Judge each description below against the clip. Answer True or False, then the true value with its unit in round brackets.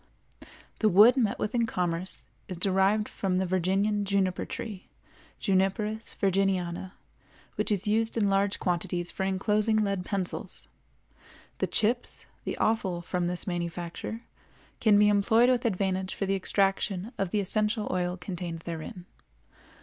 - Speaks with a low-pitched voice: False (195 Hz)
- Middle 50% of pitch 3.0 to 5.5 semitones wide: False (2.6 semitones)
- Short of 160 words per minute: True (140 wpm)